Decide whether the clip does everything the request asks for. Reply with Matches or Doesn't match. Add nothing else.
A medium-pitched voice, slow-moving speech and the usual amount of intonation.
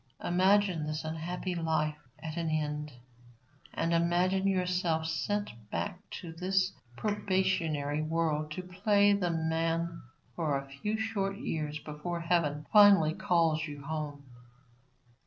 Matches